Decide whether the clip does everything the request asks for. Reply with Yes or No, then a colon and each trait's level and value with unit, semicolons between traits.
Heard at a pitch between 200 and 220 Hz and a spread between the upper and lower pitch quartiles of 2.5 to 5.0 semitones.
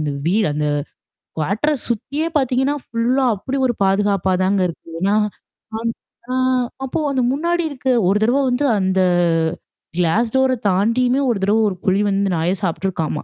No: high, 215 Hz; wide, 5.4 semitones